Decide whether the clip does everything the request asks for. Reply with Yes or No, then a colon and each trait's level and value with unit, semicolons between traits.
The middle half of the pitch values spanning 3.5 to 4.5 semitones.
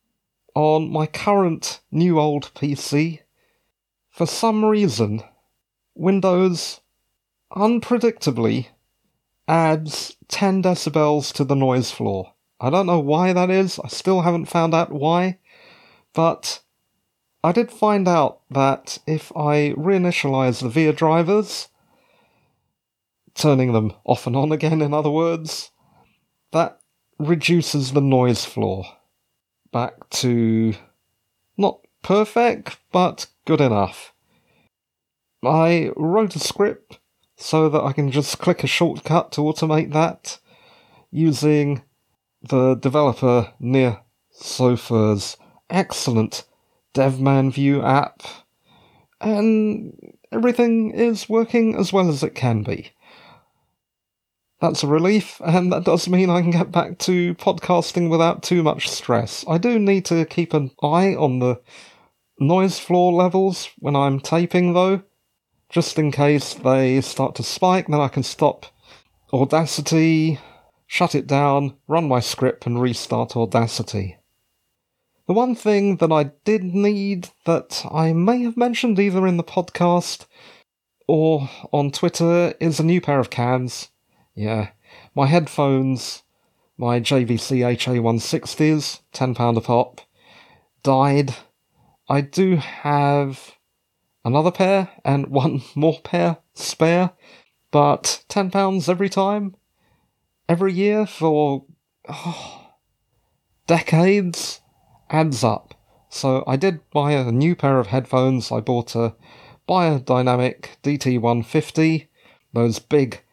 No: average, 5.2 semitones